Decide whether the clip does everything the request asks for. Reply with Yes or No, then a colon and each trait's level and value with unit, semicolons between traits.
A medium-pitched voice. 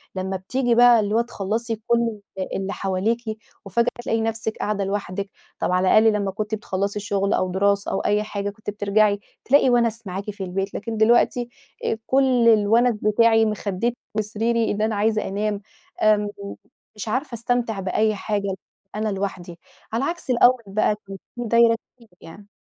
No: high, 215 Hz